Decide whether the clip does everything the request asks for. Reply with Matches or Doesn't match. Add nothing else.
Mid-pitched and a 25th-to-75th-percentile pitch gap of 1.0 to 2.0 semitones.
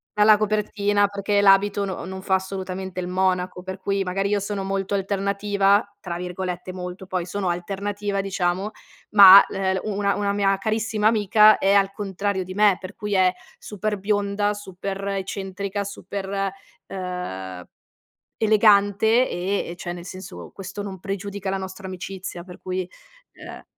Doesn't match